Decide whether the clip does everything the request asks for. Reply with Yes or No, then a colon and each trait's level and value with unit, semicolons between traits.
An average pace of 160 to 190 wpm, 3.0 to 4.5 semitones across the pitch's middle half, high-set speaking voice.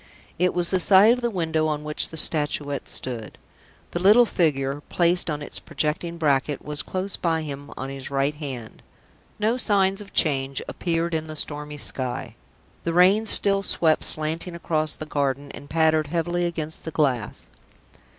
No: average, 170 wpm; average, 3.5 semitones; medium, 155 Hz